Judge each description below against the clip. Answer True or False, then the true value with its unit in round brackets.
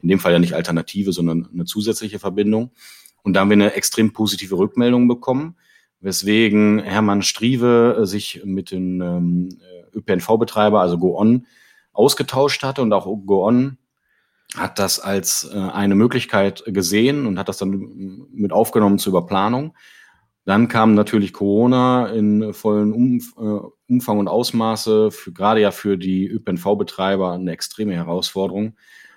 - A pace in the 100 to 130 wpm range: False (140 wpm)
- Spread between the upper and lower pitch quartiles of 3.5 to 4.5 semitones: False (2.7 semitones)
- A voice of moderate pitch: False (105 Hz)